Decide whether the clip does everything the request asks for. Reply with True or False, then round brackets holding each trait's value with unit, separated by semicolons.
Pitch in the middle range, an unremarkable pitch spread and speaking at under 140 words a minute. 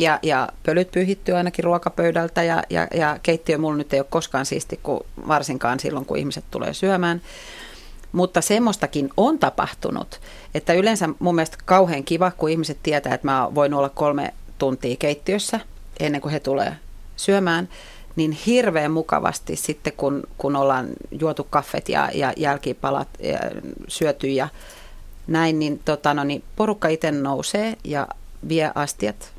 False (155 Hz; 3.3 semitones; 150 wpm)